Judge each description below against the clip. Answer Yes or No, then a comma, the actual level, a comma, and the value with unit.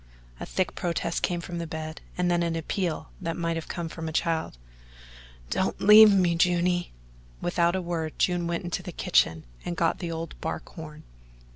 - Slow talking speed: No, average, 185 wpm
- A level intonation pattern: Yes, narrow, 1.4 semitones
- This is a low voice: No, medium, 170 Hz